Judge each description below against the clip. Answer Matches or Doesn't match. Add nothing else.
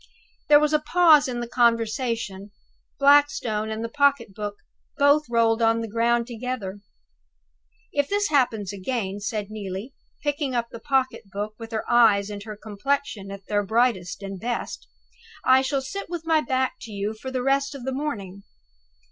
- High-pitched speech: Matches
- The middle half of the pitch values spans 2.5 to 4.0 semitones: Doesn't match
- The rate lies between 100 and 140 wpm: Doesn't match